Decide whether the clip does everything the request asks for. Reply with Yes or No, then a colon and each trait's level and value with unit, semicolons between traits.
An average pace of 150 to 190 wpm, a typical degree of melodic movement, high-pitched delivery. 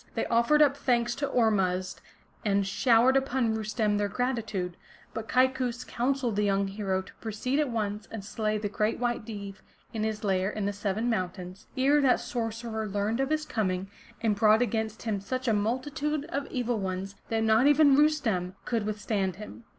Yes: average, 180 wpm; average, 3.7 semitones; high, 220 Hz